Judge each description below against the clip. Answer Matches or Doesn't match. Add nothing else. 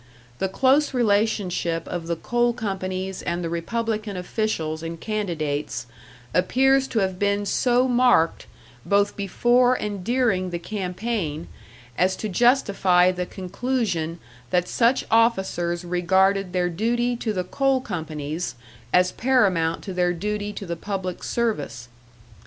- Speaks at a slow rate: Matches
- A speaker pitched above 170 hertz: Matches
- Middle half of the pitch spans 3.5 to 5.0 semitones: Matches